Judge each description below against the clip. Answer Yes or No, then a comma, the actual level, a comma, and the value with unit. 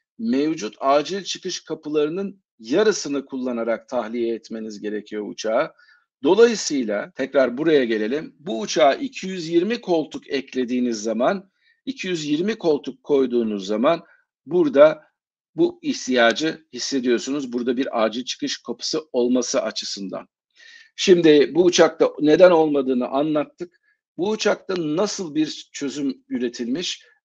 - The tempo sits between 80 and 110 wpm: Yes, average, 105 wpm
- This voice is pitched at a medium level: Yes, medium, 165 Hz